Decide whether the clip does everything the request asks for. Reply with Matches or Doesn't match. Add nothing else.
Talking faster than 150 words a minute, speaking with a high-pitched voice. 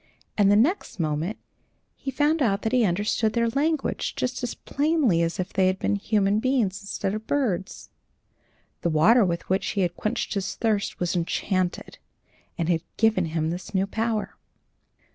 Matches